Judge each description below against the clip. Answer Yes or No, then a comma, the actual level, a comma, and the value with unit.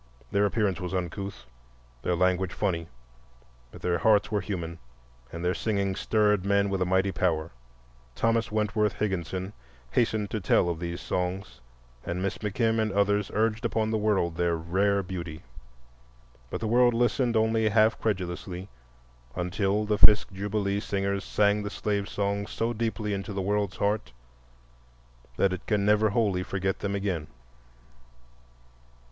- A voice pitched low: Yes, low, 100 Hz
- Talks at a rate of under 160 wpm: Yes, average, 150 wpm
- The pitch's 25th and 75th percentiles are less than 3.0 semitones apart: Yes, narrow, 2.5 semitones